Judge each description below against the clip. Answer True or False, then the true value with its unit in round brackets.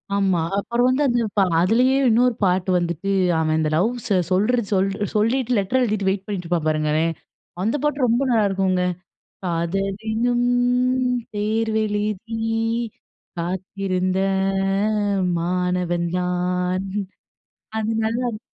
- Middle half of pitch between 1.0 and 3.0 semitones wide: False (4.0 semitones)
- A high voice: True (195 Hz)